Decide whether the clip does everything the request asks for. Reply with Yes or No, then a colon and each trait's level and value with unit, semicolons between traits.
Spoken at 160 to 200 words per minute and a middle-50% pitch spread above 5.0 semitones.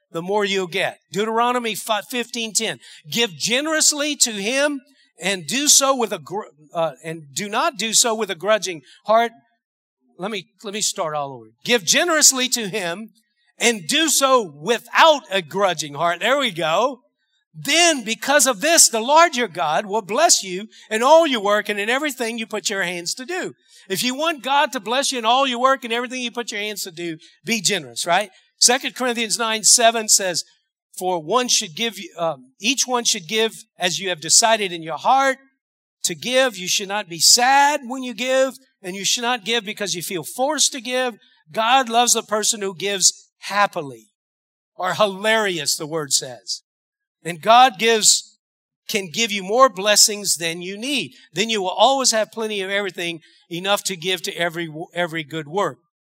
Yes: average, 190 wpm; wide, 5.4 semitones